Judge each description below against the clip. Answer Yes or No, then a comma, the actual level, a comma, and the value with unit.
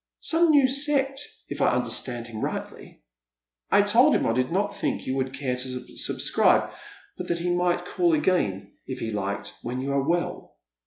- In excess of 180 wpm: Yes, average, 190 wpm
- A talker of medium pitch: Yes, medium, 155 Hz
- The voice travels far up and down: Yes, wide, 8.3 semitones